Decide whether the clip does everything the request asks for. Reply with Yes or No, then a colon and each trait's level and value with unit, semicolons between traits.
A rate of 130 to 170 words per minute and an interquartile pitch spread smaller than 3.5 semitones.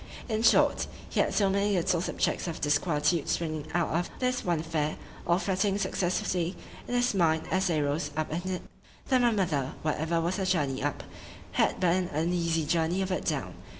No: average, 190 wpm; average, 3.1 semitones